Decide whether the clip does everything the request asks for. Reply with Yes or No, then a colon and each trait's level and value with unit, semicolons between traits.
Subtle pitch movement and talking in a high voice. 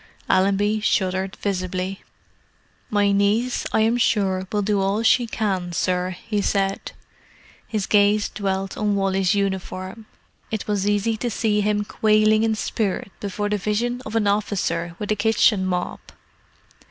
Yes: narrow, 1.9 semitones; high, 205 Hz